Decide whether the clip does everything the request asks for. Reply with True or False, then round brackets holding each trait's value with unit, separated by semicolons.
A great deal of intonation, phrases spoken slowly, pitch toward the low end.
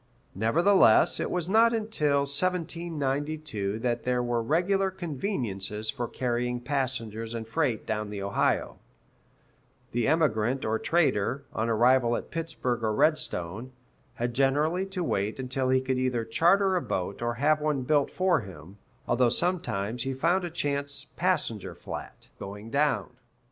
False (6.1 semitones; 145 wpm; 130 Hz)